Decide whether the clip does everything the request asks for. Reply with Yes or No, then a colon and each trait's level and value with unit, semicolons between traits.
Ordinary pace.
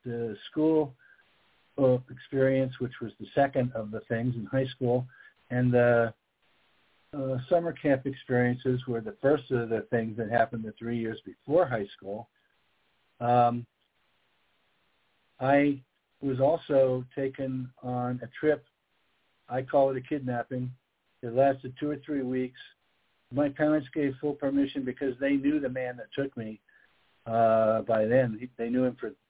Yes: average, 145 wpm